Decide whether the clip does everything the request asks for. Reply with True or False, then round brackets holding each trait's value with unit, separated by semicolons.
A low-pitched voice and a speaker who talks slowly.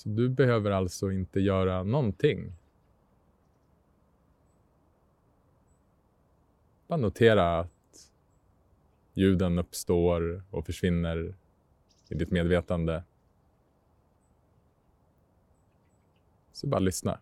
True (90 Hz; 70 wpm)